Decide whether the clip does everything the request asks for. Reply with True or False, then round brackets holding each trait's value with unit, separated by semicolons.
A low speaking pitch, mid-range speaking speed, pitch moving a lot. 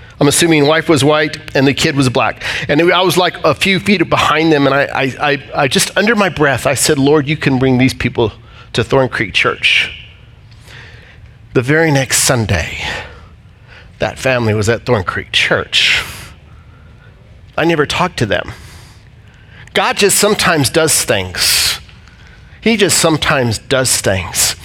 True (130 Hz; 160 wpm; 5.8 semitones)